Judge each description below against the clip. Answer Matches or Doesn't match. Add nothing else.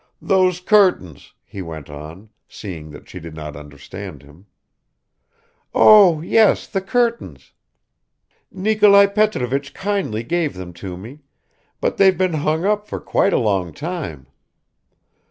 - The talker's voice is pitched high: Doesn't match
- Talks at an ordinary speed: Doesn't match